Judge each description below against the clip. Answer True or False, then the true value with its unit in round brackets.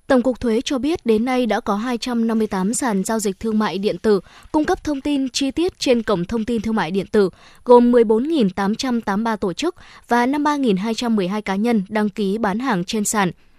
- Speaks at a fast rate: False (200 wpm)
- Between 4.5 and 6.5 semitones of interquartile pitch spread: False (3.5 semitones)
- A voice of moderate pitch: False (225 Hz)